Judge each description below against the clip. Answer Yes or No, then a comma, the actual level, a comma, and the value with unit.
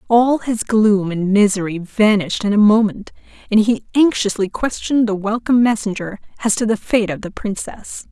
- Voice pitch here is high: Yes, high, 210 Hz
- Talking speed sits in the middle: Yes, average, 170 wpm